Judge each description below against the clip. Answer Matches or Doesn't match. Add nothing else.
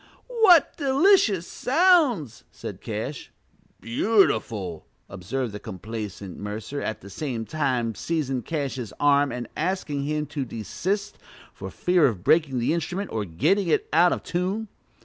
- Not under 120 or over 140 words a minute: Matches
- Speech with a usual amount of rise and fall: Doesn't match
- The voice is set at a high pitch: Doesn't match